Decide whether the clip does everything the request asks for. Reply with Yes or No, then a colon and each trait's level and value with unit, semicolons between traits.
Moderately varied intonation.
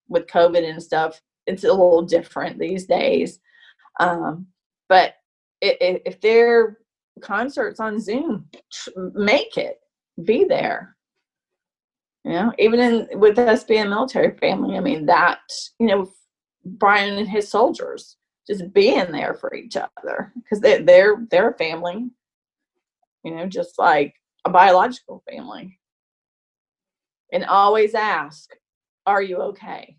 No: wide, 5.7 semitones